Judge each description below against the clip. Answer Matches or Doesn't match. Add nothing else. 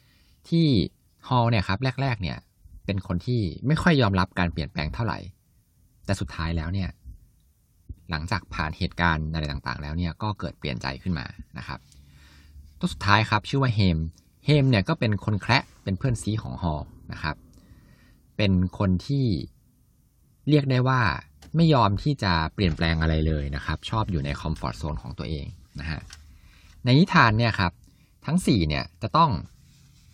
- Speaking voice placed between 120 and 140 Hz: Doesn't match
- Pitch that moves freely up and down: Matches